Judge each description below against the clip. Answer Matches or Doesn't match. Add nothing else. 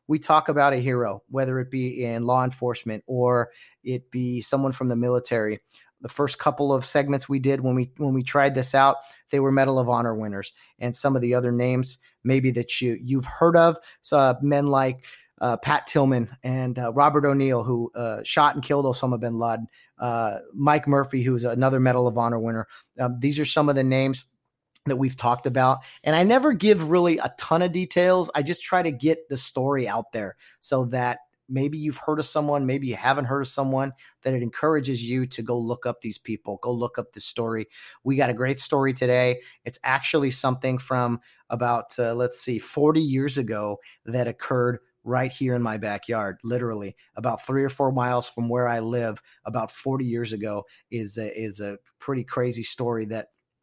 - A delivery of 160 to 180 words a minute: Doesn't match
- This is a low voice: Matches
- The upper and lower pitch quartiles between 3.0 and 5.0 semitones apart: Doesn't match